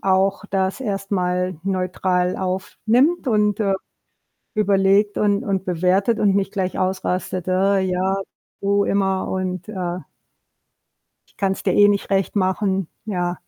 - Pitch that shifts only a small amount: Yes, narrow, 1.5 semitones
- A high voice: Yes, high, 195 Hz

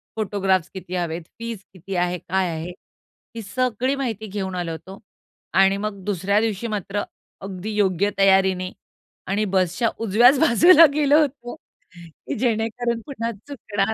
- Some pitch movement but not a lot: Yes, average, 3.7 semitones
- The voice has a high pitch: Yes, high, 200 Hz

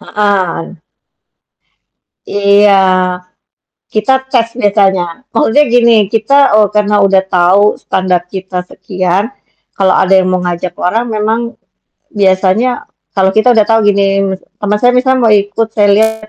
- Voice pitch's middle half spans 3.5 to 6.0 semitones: No, average, 2.8 semitones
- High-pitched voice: Yes, high, 205 Hz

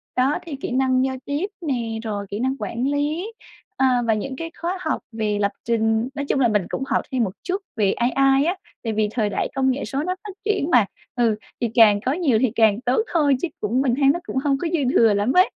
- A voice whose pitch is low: No, very high, 260 Hz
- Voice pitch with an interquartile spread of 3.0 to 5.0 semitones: Yes, average, 4.3 semitones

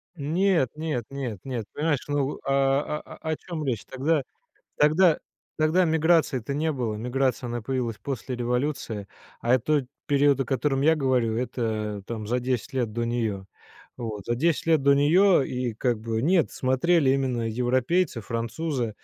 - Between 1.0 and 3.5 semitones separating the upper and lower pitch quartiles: No, average, 4.3 semitones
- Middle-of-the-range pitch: No, low, 130 Hz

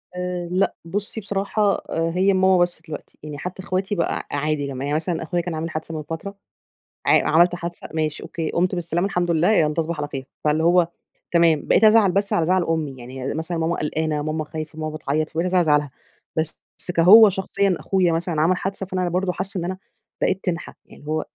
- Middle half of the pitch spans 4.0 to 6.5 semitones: No, average, 2.9 semitones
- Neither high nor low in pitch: Yes, medium, 170 Hz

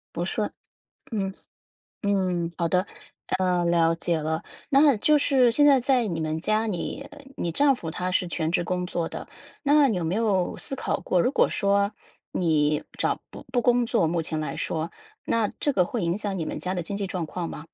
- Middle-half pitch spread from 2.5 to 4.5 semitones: No, wide, 5.4 semitones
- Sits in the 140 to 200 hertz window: Yes, medium, 185 Hz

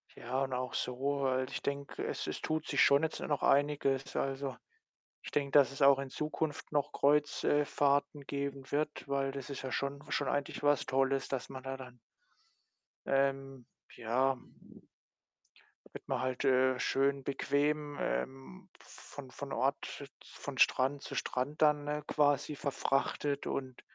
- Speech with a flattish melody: Yes, narrow, 1.4 semitones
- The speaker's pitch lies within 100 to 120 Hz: No, medium, 140 Hz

